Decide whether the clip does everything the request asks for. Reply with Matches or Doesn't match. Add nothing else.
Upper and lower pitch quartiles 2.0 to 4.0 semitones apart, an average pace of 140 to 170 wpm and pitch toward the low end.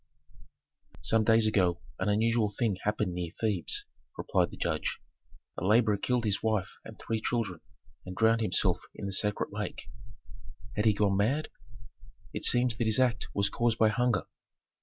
Matches